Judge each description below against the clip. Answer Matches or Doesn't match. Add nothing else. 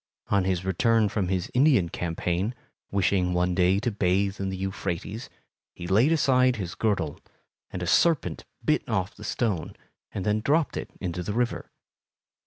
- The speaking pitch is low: Matches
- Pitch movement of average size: Matches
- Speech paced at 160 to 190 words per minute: Matches